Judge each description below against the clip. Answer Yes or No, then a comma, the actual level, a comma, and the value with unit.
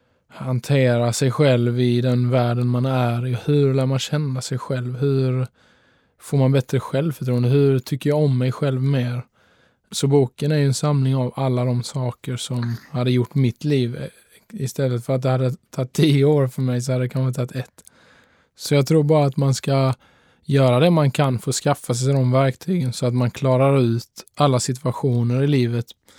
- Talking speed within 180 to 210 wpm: Yes, average, 190 wpm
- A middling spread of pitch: No, narrow, 1.9 semitones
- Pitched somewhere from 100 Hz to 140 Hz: Yes, low, 130 Hz